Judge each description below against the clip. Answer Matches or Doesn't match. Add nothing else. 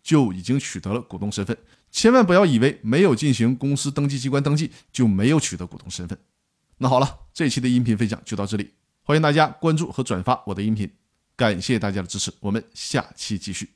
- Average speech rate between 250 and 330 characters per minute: Doesn't match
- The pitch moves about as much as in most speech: Doesn't match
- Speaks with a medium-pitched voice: Doesn't match